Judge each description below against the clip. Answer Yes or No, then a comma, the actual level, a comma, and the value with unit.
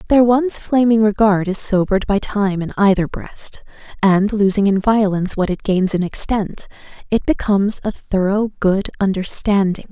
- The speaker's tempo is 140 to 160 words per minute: Yes, average, 155 wpm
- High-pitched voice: Yes, high, 200 Hz